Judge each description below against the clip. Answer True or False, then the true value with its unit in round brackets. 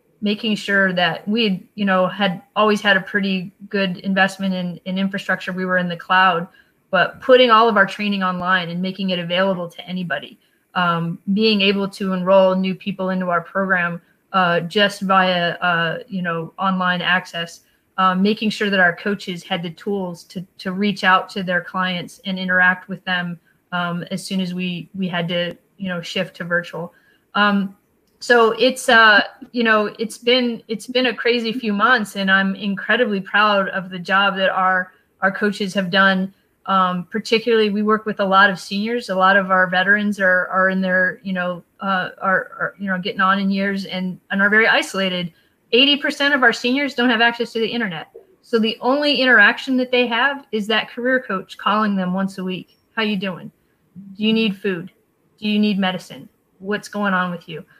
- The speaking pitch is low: False (195 Hz)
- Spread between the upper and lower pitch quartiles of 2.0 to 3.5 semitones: True (2.6 semitones)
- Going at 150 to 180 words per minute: False (195 wpm)